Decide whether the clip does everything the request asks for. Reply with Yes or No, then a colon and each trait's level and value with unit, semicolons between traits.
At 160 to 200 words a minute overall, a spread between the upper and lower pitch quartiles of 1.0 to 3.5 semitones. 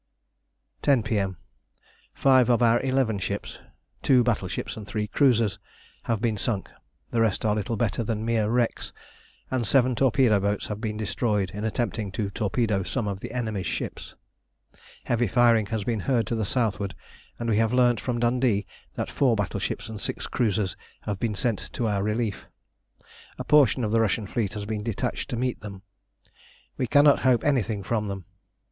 Yes: average, 175 wpm; average, 2.8 semitones